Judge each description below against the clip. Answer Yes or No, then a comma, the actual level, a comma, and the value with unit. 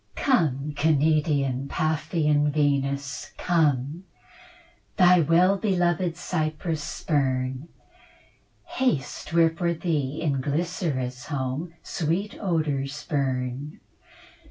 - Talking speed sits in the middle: No, slow, 85 wpm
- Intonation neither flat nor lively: Yes, average, 3.5 semitones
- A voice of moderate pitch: Yes, medium, 150 Hz